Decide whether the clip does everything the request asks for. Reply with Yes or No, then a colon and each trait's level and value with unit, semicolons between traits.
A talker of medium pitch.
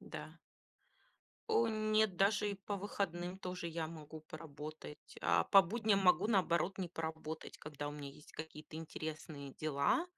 Yes: medium, 170 Hz